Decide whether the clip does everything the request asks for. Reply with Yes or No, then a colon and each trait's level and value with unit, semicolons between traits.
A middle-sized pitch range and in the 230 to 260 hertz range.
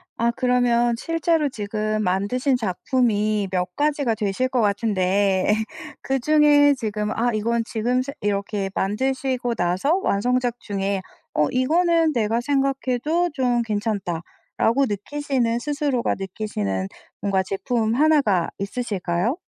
Yes: average, 4.8 semitones; high, 235 Hz